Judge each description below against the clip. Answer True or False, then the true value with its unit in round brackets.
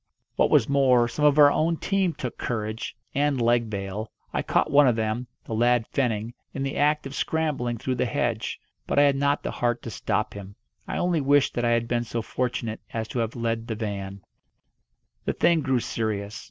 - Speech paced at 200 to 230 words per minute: True (205 wpm)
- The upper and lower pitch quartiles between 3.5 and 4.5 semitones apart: True (4.0 semitones)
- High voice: False (120 Hz)